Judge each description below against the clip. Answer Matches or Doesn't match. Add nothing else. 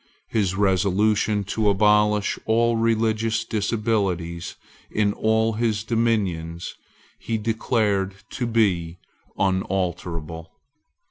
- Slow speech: Matches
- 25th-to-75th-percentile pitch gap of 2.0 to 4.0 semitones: Matches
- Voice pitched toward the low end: Matches